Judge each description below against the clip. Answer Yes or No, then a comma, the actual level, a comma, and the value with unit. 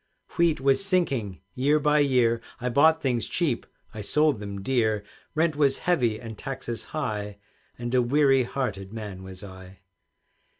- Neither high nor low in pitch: No, low, 125 Hz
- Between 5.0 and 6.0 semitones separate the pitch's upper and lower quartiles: Yes, wide, 5.5 semitones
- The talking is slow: No, average, 155 wpm